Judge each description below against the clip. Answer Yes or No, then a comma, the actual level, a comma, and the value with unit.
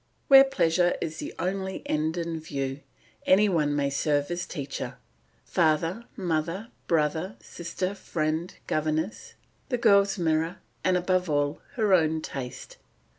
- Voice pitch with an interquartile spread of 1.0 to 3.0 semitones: No, average, 3.4 semitones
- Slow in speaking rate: Yes, slow, 130 wpm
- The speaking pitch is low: No, medium, 165 Hz